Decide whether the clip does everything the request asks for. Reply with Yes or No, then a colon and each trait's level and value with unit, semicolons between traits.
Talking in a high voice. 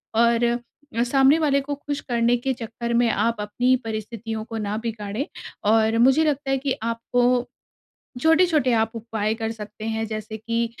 Yes: high, 235 Hz